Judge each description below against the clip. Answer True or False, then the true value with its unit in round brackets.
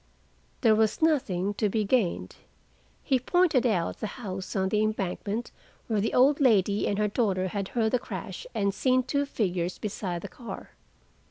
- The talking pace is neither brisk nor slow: True (170 wpm)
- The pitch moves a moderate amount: True (4.4 semitones)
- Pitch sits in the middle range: False (215 Hz)